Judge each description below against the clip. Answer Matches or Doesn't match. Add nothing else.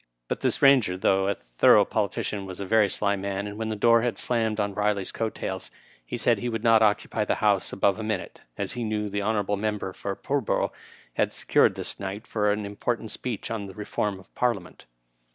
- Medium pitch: Doesn't match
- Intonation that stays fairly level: Matches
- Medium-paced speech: Doesn't match